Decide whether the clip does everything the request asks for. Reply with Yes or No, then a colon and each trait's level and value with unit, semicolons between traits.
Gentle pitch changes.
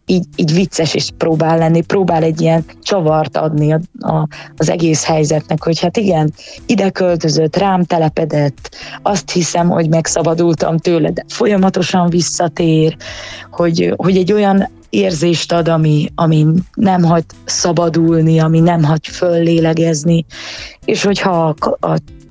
Yes: narrow, 2.1 semitones